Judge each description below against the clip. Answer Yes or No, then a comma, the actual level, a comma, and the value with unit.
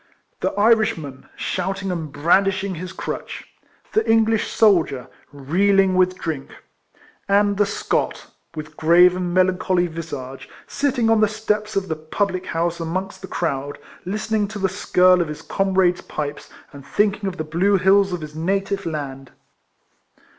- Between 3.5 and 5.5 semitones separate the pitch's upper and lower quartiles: Yes, average, 3.8 semitones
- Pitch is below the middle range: No, medium, 185 Hz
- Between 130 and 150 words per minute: Yes, average, 145 wpm